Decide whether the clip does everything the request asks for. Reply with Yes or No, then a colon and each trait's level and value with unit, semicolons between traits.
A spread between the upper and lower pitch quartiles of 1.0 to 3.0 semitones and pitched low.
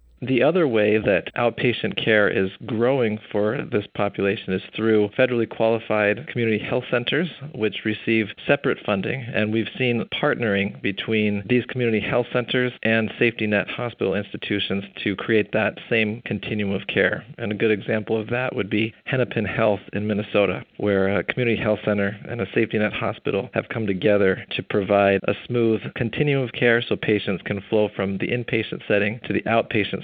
Yes: narrow, 2.6 semitones; low, 110 Hz